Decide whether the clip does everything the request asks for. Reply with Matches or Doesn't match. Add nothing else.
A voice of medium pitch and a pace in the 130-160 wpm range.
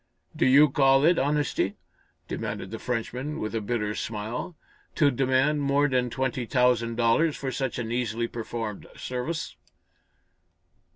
Doesn't match